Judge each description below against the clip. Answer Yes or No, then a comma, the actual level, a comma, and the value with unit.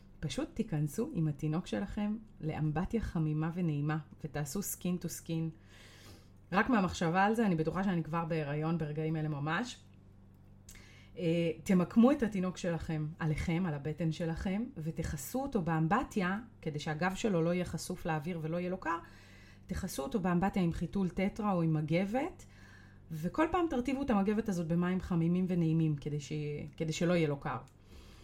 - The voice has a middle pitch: Yes, medium, 165 Hz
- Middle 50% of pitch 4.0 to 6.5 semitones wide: No, average, 3.5 semitones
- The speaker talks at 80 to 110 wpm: No, average, 145 wpm